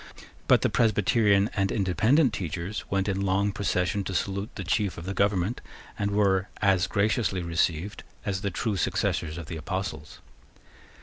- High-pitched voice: No, low, 100 Hz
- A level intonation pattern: Yes, narrow, 2.1 semitones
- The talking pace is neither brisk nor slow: Yes, average, 160 wpm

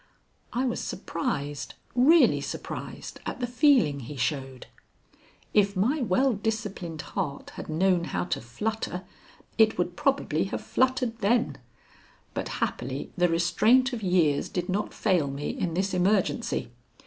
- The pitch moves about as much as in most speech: No, wide, 6.3 semitones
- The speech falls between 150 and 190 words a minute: No, slow, 135 wpm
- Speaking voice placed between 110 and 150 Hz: No, high, 190 Hz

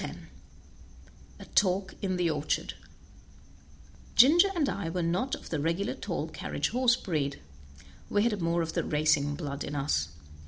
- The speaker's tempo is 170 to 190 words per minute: No, average, 155 wpm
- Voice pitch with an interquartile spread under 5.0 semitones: No, average, 5.3 semitones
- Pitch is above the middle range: No, medium, 170 Hz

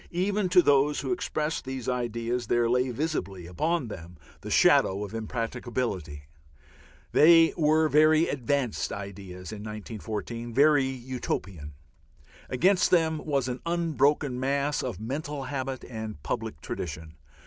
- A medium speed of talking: No, slow, 125 wpm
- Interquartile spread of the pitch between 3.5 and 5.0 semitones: No, wide, 5.6 semitones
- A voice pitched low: Yes, low, 130 Hz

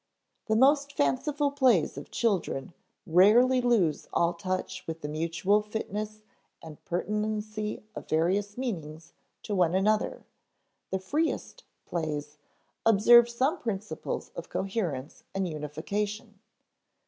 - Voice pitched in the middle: No, high, 205 Hz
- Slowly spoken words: Yes, slow, 110 wpm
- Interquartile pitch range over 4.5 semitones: Yes, wide, 5.4 semitones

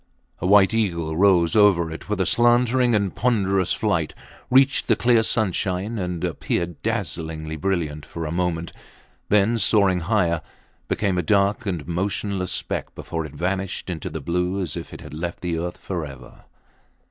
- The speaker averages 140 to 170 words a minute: Yes, average, 160 wpm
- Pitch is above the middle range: No, very low, 90 Hz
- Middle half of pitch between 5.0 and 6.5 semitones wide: No, average, 3.4 semitones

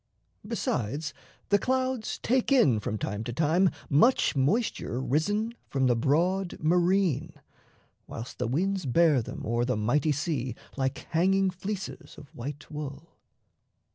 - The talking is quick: No, slow, 135 wpm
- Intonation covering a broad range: Yes, wide, 6.4 semitones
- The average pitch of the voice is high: No, medium, 155 Hz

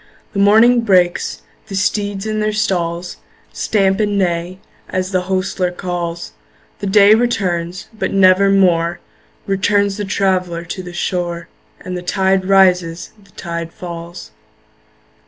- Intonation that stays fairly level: Yes, narrow, 2.3 semitones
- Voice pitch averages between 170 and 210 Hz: Yes, medium, 185 Hz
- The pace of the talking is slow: Yes, slow, 130 wpm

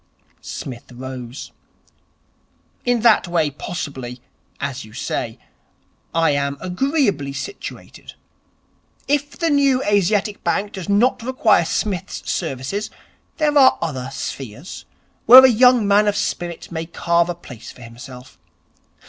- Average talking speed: No, slow, 125 wpm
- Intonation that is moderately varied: No, wide, 8.5 semitones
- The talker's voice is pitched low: No, medium, 175 Hz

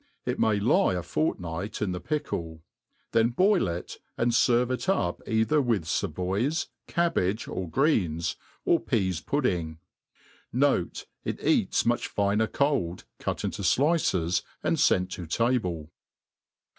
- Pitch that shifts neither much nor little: No, wide, 6.7 semitones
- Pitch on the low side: Yes, low, 105 Hz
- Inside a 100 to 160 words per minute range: Yes, slow, 135 wpm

